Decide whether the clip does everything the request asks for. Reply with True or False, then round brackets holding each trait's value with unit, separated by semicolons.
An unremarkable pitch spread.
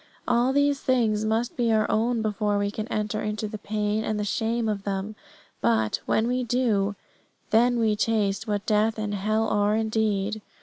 False (1.4 semitones)